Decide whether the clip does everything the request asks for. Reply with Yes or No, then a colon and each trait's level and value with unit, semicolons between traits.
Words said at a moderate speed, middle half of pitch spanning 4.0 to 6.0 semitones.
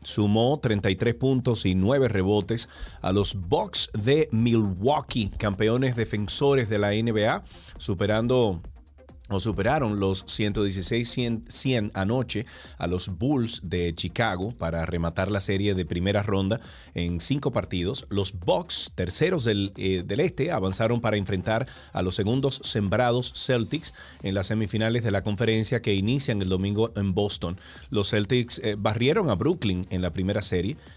No: average, 145 wpm; average, 3.6 semitones